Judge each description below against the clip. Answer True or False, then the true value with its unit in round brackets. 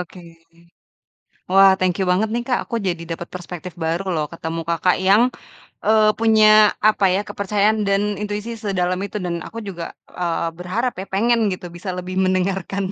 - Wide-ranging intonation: False (2.9 semitones)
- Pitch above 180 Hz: True (190 Hz)